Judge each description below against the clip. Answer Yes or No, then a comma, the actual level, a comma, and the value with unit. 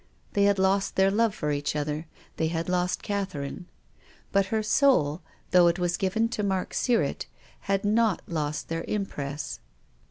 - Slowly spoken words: No, average, 160 wpm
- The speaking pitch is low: No, high, 190 Hz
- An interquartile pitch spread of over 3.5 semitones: Yes, average, 4.0 semitones